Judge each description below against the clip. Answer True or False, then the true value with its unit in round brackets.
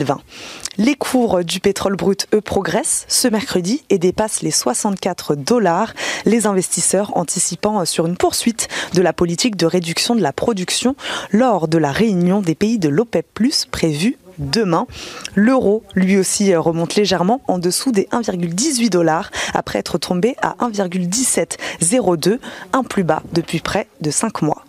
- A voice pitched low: False (195 Hz)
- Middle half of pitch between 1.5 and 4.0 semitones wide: False (4.8 semitones)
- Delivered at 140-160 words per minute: True (150 wpm)